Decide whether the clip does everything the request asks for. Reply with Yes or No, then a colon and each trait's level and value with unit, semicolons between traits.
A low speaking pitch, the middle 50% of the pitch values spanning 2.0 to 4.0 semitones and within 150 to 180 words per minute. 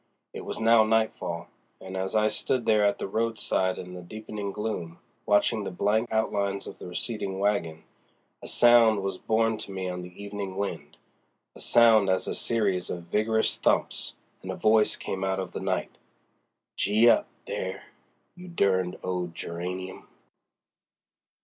Yes: low, 100 Hz; average, 2.9 semitones; average, 155 wpm